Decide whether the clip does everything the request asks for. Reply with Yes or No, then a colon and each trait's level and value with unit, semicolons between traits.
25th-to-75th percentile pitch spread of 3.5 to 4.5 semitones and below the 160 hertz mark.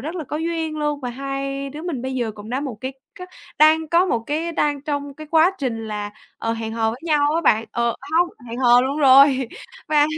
No: average, 4.2 semitones; very high, 275 Hz